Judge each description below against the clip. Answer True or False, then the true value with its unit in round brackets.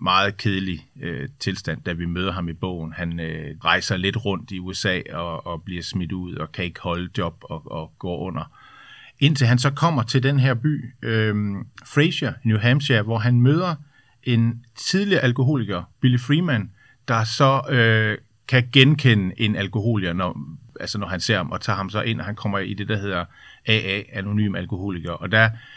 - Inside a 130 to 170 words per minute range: False (190 wpm)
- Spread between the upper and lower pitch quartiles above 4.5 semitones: True (4.9 semitones)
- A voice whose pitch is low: True (110 Hz)